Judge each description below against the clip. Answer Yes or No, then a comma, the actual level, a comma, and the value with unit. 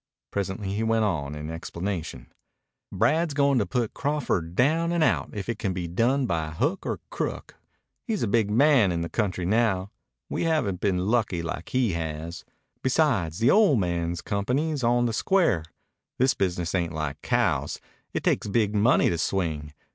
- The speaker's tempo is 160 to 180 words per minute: Yes, average, 170 wpm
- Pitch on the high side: No, low, 100 Hz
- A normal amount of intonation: No, wide, 6.7 semitones